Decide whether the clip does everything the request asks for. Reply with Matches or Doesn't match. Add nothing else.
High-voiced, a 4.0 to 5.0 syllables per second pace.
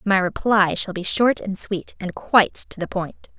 Matches